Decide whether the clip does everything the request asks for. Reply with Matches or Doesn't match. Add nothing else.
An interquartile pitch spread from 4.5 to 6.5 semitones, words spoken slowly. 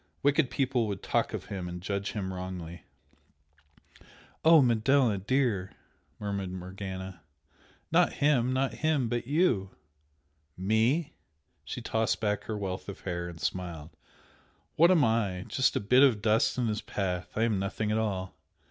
Doesn't match